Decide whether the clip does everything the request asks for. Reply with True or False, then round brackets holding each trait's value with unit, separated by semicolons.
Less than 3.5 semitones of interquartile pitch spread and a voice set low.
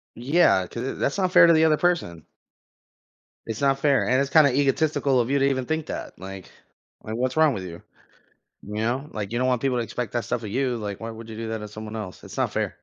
False (4.3 semitones; 125 Hz)